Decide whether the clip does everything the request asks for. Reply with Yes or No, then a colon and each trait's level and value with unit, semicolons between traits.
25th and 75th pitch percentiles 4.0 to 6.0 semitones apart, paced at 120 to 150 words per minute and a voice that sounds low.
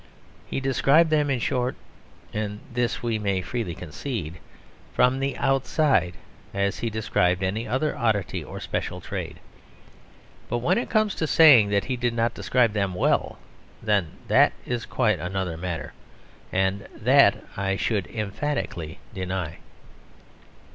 Yes: average, 5.0 semitones; average, 140 wpm; low, 110 Hz